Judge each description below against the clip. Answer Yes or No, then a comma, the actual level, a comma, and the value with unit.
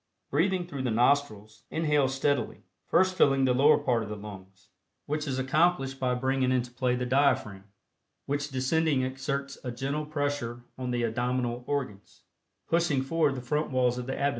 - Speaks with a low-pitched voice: Yes, low, 130 Hz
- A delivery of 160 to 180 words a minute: Yes, average, 170 wpm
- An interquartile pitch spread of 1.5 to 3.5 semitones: Yes, narrow, 2.6 semitones